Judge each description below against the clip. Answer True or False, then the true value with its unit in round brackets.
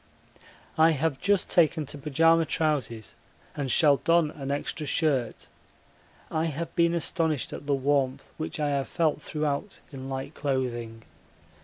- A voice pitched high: False (150 Hz)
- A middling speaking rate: True (145 wpm)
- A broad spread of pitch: False (3.2 semitones)